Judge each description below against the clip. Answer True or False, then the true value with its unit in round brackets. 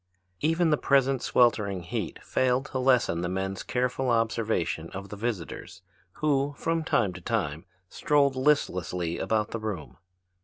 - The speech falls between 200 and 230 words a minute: False (145 wpm)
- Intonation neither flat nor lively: False (6.3 semitones)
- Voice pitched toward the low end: True (115 Hz)